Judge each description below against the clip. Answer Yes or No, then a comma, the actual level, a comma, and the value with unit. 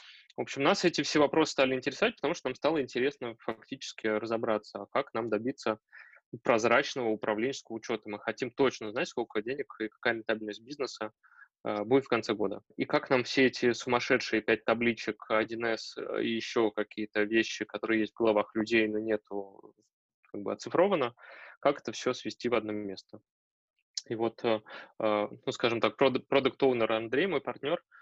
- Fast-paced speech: Yes, fast, 165 wpm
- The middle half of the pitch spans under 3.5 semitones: Yes, average, 2.8 semitones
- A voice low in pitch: Yes, low, 115 Hz